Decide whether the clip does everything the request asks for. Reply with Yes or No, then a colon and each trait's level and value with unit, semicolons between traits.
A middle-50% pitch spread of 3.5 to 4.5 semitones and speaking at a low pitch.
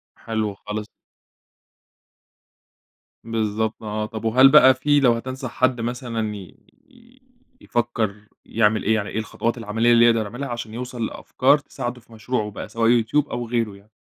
No: narrow, 2.4 semitones; low, 115 Hz